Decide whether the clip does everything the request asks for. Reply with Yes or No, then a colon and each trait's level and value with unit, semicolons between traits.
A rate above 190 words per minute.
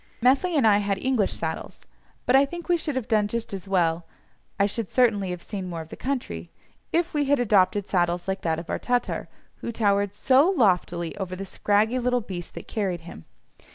Yes: fast, 205 wpm